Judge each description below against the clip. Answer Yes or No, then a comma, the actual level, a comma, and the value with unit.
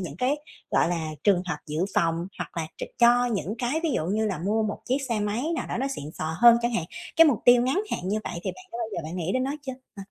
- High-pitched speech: Yes, high, 215 Hz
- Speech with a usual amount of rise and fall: No, wide, 6.1 semitones